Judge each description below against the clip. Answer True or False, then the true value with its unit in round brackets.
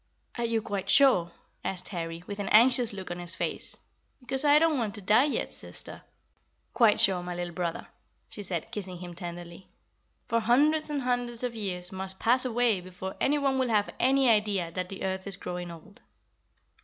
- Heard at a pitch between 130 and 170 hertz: False (205 Hz)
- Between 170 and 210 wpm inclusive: True (185 wpm)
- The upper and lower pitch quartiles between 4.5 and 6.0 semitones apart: True (5.4 semitones)